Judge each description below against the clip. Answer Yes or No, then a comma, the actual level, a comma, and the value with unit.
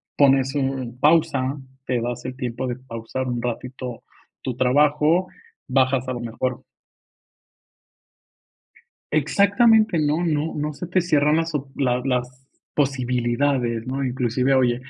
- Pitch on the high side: No, low, 130 Hz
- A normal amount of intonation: Yes, average, 3.0 semitones